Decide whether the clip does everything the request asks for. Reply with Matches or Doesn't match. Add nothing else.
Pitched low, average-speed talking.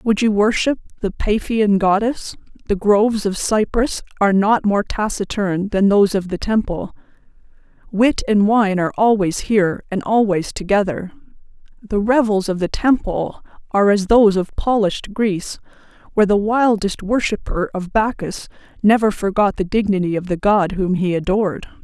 Doesn't match